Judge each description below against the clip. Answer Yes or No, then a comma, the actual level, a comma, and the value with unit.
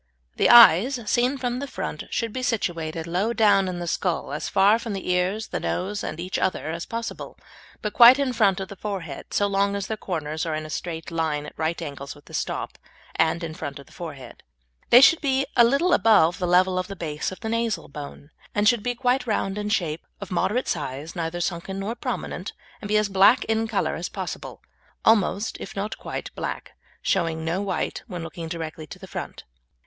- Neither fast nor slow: No, fast, 215 wpm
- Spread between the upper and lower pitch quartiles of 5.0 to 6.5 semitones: Yes, average, 5.3 semitones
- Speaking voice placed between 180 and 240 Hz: Yes, high, 190 Hz